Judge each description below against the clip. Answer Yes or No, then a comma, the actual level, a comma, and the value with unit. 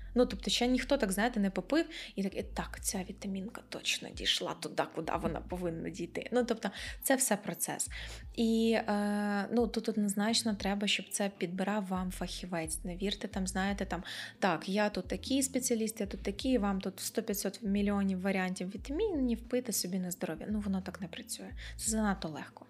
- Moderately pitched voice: No, high, 205 Hz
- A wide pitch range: No, average, 3.2 semitones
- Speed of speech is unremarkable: No, fast, 180 wpm